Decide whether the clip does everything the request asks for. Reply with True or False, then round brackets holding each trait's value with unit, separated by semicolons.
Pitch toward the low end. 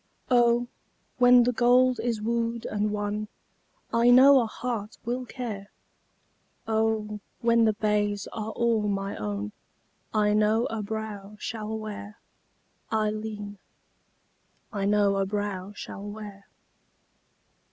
False (215 Hz)